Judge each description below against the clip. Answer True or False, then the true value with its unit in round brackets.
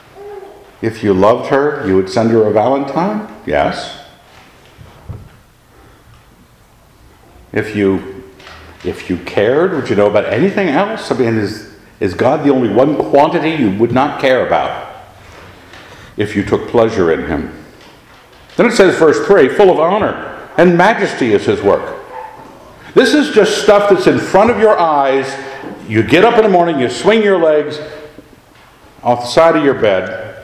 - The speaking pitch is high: False (140 Hz)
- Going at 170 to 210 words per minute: False (160 wpm)